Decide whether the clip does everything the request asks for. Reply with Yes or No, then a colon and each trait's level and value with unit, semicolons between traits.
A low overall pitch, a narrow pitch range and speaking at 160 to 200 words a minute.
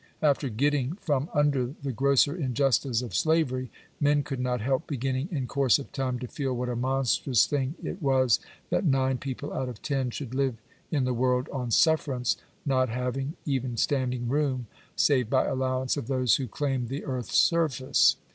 Yes: low, 130 Hz; narrow, 2.1 semitones; average, 180 wpm